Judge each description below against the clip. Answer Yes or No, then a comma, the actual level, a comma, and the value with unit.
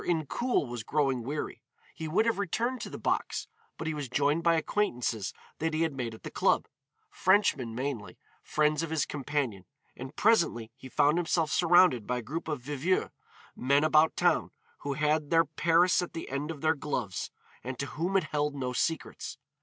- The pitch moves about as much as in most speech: Yes, average, 4.0 semitones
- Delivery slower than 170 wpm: No, average, 185 wpm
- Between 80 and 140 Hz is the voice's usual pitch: No, medium, 150 Hz